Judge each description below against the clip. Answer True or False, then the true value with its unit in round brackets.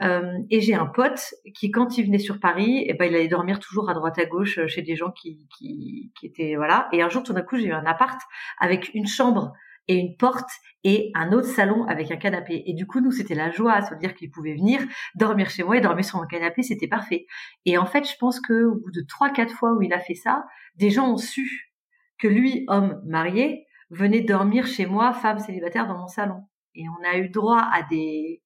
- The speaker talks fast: True (240 wpm)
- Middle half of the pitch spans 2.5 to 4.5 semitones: False (5.6 semitones)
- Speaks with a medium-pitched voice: False (205 Hz)